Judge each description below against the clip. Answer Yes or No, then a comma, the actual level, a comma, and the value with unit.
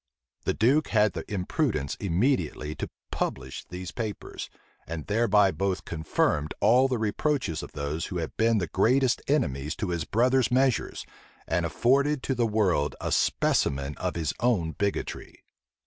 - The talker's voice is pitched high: No, low, 100 Hz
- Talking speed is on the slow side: No, average, 150 wpm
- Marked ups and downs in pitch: Yes, wide, 7.2 semitones